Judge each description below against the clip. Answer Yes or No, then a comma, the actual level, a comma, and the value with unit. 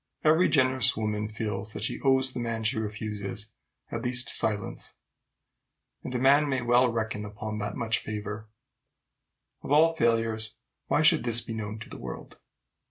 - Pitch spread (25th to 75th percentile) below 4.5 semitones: Yes, average, 3.2 semitones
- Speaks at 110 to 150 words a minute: No, average, 165 wpm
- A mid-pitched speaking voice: No, low, 115 Hz